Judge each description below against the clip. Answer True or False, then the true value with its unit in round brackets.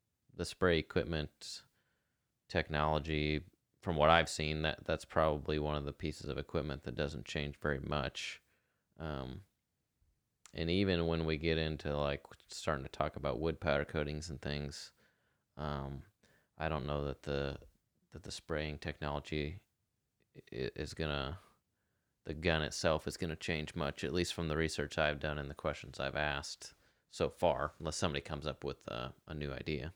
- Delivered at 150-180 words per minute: True (160 wpm)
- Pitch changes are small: True (1.9 semitones)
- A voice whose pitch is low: True (75 Hz)